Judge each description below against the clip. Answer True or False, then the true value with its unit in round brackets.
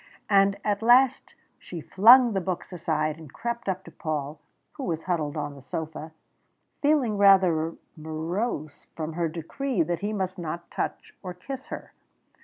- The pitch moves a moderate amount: True (4.6 semitones)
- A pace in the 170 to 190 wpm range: False (160 wpm)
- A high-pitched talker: False (175 Hz)